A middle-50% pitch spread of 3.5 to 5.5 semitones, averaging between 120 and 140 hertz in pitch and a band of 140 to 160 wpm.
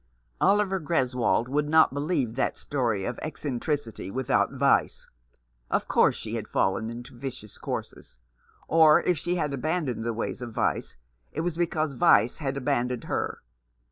Yes: average, 4.7 semitones; low, 135 Hz; average, 150 wpm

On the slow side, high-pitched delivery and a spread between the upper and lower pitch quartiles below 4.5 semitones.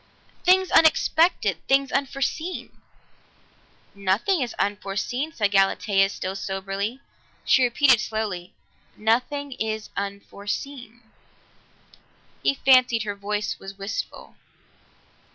No: slow, 90 wpm; high, 220 Hz; wide, 5.4 semitones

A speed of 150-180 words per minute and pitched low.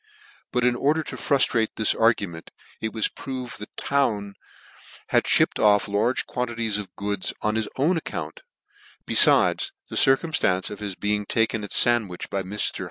Yes: average, 165 wpm; low, 110 Hz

